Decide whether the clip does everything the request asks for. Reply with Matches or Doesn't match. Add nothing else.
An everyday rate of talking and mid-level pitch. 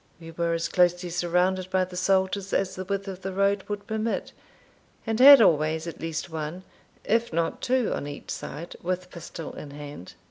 Matches